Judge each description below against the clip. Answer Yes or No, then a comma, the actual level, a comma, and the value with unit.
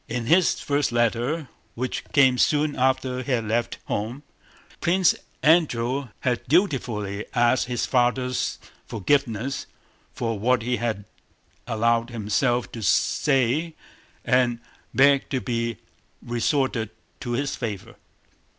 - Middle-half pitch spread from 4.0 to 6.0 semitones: No, average, 2.8 semitones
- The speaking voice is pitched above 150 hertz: No, low, 125 Hz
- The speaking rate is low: Yes, slow, 115 wpm